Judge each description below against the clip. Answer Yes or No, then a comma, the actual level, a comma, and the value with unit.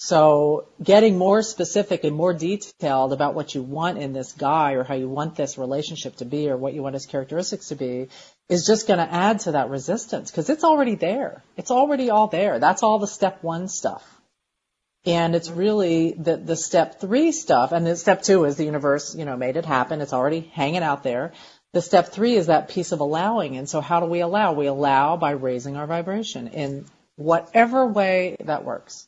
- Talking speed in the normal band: No, fast, 210 wpm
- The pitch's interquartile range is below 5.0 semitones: No, wide, 5.4 semitones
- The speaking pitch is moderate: Yes, medium, 165 Hz